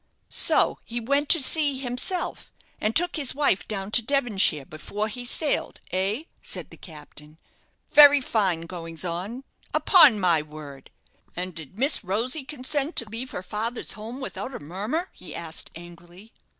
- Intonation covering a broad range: Yes, wide, 7.5 semitones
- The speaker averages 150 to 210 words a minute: Yes, average, 155 wpm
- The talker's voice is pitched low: No, high, 215 Hz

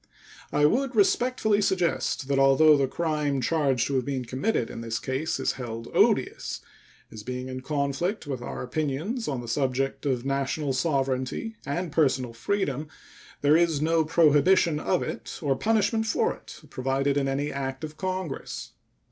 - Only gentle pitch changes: No, average, 4.2 semitones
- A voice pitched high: No, medium, 145 Hz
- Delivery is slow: No, average, 160 wpm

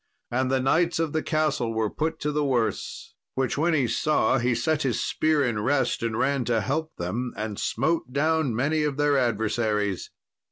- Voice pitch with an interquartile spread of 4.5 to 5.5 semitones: Yes, average, 4.9 semitones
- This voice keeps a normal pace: Yes, average, 190 wpm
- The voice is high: No, low, 135 Hz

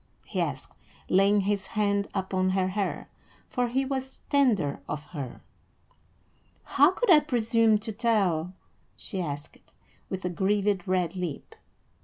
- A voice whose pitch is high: Yes, high, 200 Hz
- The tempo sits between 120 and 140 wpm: Yes, slow, 135 wpm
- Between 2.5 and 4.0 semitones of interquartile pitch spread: Yes, average, 3.7 semitones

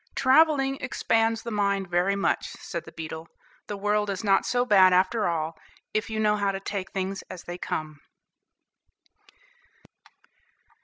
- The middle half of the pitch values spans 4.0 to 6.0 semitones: No, average, 3.2 semitones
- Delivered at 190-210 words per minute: No, average, 150 wpm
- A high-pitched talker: Yes, high, 200 Hz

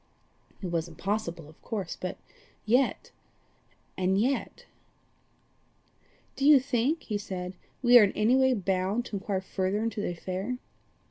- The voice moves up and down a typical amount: Yes, average, 4.6 semitones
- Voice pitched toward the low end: No, high, 205 Hz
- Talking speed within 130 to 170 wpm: Yes, average, 140 wpm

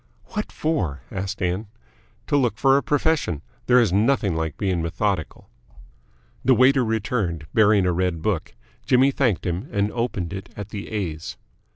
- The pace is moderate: Yes, average, 160 wpm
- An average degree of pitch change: No, wide, 5.9 semitones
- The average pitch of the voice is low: Yes, low, 100 Hz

